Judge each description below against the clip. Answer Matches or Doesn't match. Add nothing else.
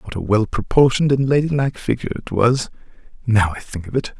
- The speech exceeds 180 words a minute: Matches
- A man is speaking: Matches